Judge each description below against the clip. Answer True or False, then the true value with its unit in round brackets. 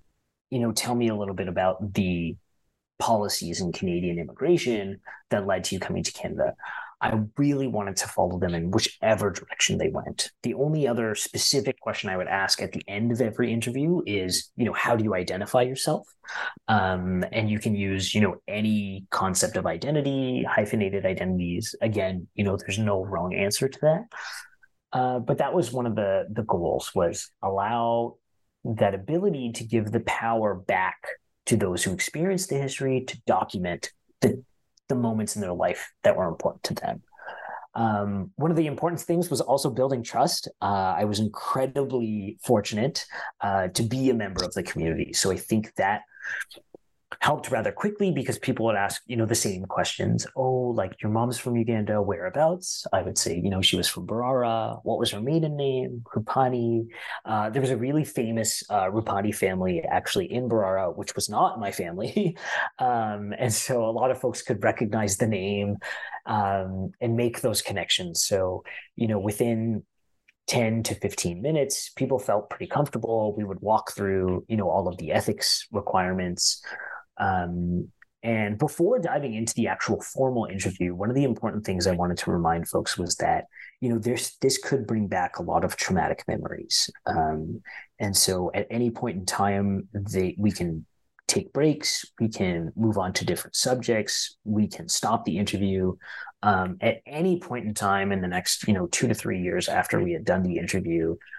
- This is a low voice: True (110 Hz)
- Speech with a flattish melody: False (4.6 semitones)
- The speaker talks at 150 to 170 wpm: False (180 wpm)